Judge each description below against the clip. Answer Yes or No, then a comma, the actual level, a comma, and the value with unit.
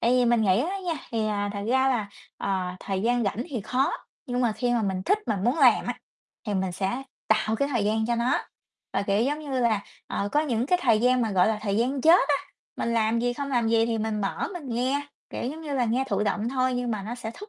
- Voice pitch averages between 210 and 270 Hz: Yes, high, 235 Hz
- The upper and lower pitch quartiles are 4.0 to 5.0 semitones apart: No, average, 3.4 semitones